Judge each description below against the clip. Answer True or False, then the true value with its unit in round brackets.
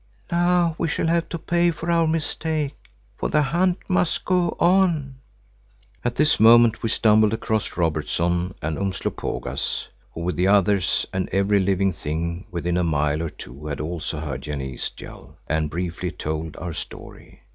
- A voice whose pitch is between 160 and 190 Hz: False (95 Hz)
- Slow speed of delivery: False (160 wpm)